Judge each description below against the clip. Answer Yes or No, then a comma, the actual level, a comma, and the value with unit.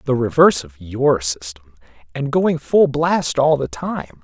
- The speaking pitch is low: Yes, low, 125 Hz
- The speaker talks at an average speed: Yes, average, 170 wpm